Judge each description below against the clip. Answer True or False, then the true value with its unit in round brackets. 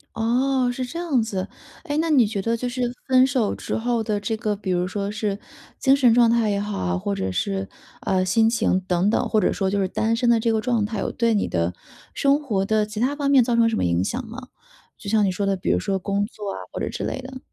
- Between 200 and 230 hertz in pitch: True (220 Hz)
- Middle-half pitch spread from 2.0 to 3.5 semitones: False (3.9 semitones)